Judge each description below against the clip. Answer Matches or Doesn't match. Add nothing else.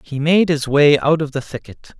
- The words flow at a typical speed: Doesn't match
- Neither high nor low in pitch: Matches